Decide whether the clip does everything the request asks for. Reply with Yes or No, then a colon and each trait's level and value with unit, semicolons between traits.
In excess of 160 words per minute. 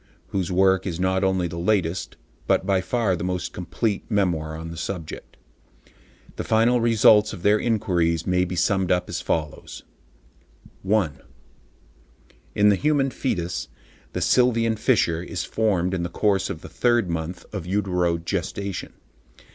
No: average, 145 wpm